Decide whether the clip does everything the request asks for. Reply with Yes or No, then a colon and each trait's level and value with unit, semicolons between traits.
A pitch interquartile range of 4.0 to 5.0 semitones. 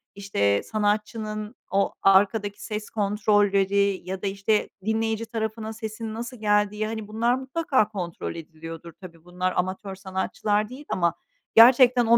No: narrow, 2.4 semitones